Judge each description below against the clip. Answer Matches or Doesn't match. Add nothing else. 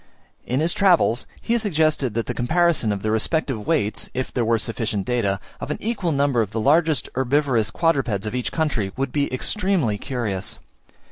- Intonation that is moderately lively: Doesn't match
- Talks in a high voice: Doesn't match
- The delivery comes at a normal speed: Matches